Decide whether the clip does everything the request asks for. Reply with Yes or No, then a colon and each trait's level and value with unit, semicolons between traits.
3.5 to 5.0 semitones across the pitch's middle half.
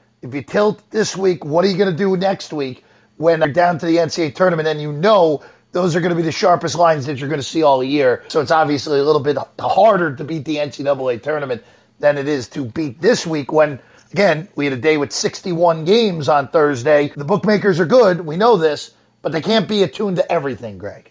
Yes: average, 4.2 semitones